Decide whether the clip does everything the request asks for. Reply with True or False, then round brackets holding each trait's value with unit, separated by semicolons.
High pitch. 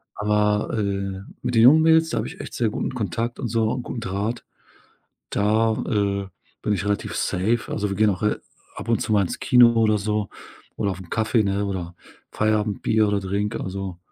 False (105 Hz)